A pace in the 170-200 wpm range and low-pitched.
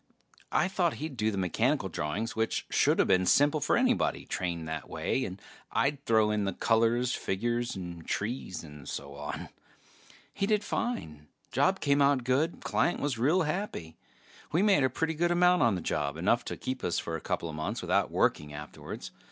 Yes: average, 185 wpm; low, 115 Hz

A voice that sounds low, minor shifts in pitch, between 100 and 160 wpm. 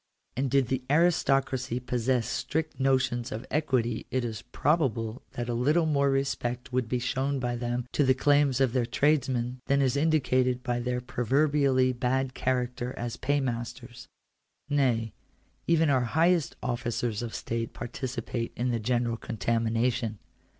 Yes: low, 125 Hz; narrow, 2.3 semitones; average, 145 wpm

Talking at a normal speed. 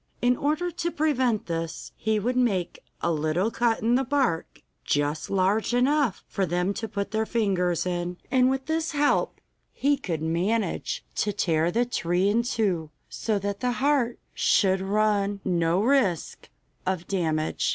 Yes: average, 160 wpm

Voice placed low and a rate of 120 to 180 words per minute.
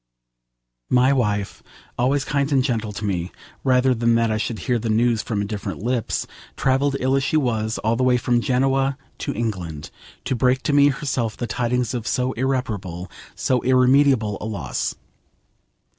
Yes: low, 120 Hz; average, 170 wpm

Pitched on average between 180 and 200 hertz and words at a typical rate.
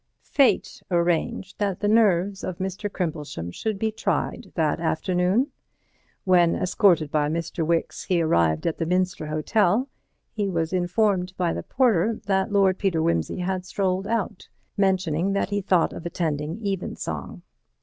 Yes: medium, 185 Hz; average, 150 wpm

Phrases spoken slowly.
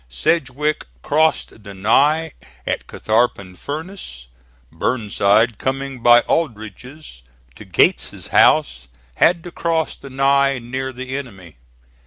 Yes: slow, 110 wpm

